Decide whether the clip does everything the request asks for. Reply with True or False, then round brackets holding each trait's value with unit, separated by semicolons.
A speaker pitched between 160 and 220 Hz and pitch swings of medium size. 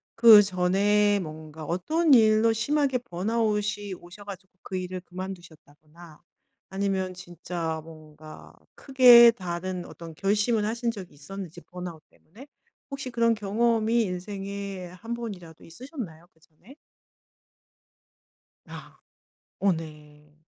True (190 Hz; 4.6 semitones)